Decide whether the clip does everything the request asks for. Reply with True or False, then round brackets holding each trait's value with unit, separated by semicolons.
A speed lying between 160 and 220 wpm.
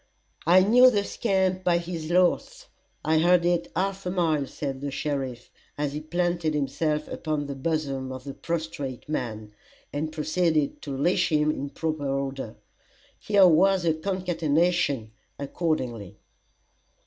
False (140 wpm)